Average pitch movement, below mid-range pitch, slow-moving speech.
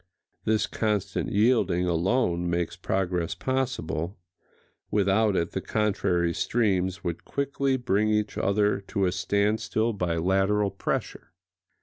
Yes: average, 3.4 semitones; low, 100 Hz; slow, 115 wpm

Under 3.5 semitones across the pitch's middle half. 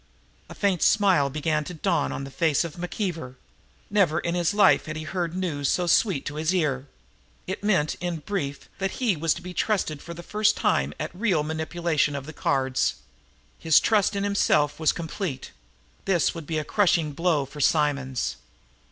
No: average, 3.9 semitones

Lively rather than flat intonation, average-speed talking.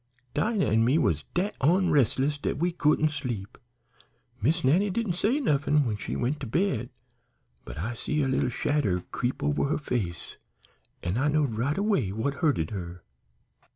Yes: wide, 6.2 semitones; average, 165 wpm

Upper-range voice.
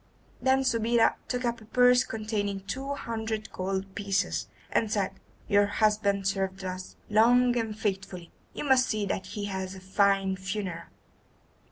Yes: high, 205 Hz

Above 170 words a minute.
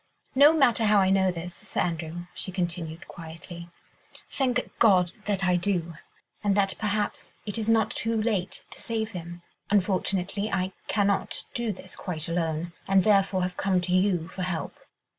No: average, 165 wpm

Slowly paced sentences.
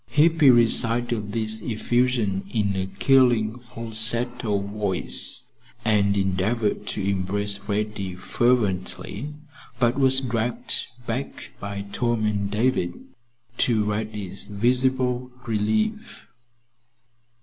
Yes: slow, 95 wpm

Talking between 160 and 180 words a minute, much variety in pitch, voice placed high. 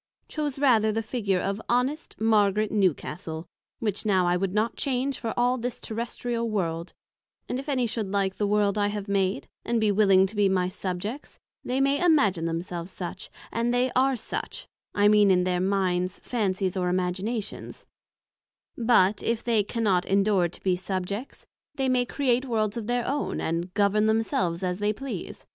No: average, 175 wpm; average, 4.1 semitones; high, 210 Hz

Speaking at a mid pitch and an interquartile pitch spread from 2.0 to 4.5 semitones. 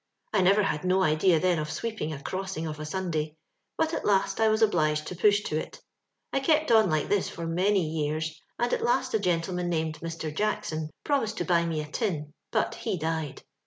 No: medium, 175 Hz; average, 4.9 semitones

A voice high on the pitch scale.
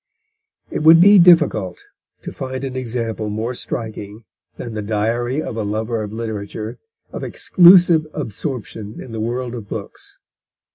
No: low, 115 Hz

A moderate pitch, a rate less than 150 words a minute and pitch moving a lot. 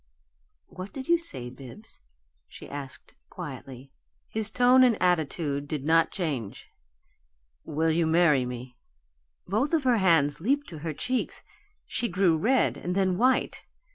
Yes: medium, 170 Hz; average, 140 wpm; wide, 7.5 semitones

